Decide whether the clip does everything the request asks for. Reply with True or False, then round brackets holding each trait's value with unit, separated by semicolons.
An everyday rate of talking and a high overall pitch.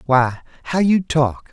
False (160 wpm; 150 Hz)